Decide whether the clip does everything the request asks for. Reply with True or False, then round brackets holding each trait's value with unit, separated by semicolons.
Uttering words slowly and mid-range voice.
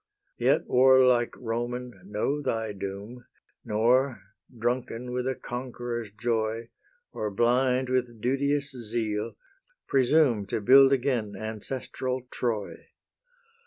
False (100 wpm; 120 Hz)